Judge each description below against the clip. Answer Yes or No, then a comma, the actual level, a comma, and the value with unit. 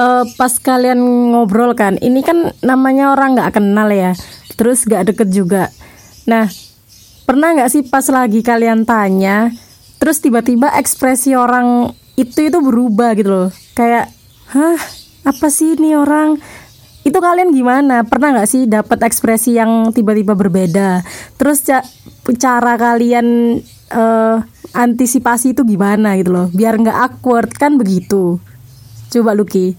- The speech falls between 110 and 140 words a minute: Yes, average, 135 wpm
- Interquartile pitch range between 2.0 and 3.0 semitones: No, average, 3.6 semitones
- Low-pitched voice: No, high, 235 Hz